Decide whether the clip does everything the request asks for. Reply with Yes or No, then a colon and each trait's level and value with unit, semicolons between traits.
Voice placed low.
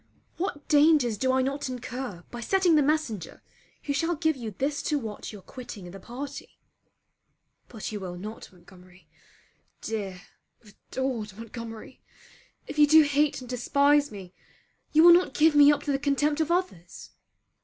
No: very high, 260 Hz